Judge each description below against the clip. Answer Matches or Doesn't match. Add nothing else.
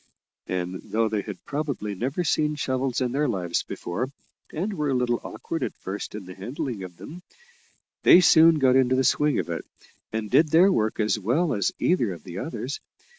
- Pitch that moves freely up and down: Matches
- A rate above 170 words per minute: Matches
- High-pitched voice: Doesn't match